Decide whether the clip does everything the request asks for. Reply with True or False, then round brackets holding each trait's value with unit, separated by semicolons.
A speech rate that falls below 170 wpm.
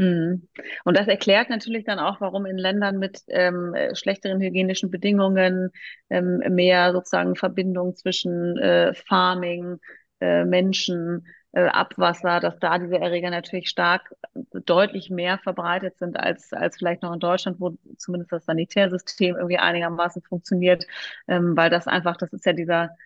True (145 wpm)